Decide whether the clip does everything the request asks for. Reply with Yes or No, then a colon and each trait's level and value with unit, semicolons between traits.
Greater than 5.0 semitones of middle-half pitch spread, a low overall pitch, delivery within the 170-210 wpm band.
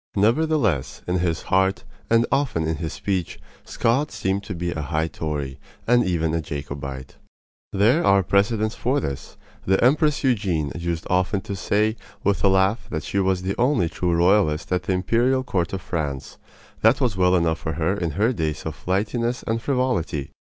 Yes: wide, 5.6 semitones; very low, 95 Hz; average, 180 wpm